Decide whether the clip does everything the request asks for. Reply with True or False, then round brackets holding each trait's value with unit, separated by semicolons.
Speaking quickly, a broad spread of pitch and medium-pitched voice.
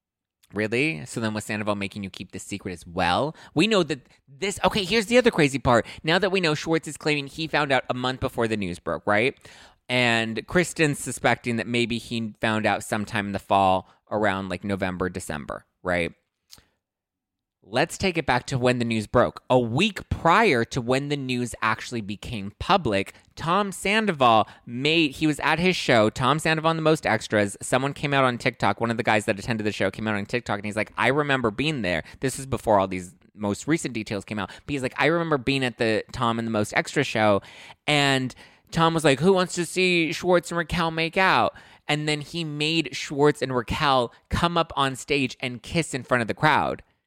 False (215 wpm; 6.6 semitones; 125 Hz)